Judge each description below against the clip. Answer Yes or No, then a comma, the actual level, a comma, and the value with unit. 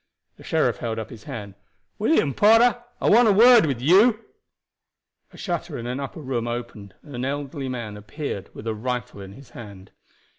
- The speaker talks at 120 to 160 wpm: No, average, 185 wpm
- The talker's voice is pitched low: Yes, low, 130 Hz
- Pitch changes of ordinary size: No, wide, 7.5 semitones